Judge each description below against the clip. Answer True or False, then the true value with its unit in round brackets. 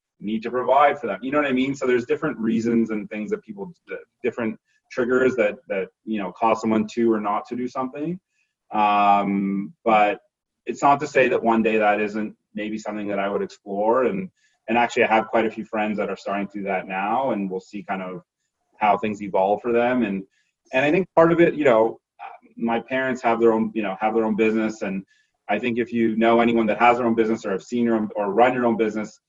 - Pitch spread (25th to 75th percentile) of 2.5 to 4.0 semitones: True (2.8 semitones)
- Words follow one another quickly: True (240 wpm)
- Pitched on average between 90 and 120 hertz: True (115 Hz)